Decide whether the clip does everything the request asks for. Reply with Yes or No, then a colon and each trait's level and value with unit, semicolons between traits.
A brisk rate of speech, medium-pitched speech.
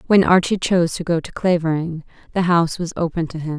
Yes: fast, 220 wpm; medium, 170 Hz